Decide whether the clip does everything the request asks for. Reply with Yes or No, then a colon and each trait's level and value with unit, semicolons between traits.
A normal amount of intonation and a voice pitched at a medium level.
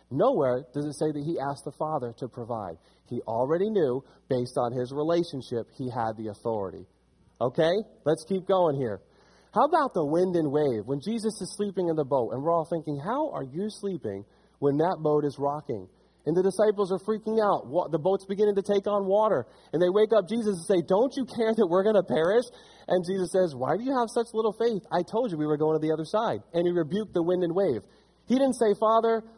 No: wide, 6.3 semitones; medium, 180 Hz